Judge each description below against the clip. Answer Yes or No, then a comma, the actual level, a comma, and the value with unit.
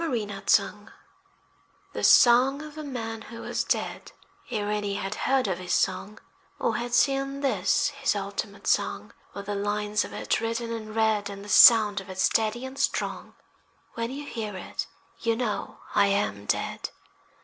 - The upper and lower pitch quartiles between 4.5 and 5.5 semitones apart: No, average, 3.4 semitones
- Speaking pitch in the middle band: No, high, 220 Hz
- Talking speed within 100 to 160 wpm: No, average, 170 wpm